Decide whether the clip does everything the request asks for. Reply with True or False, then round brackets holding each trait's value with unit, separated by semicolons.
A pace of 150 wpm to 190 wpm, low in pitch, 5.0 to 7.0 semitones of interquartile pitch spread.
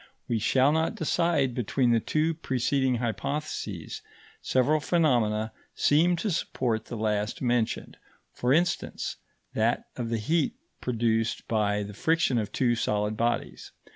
False (135 wpm; 125 Hz; 5.4 semitones)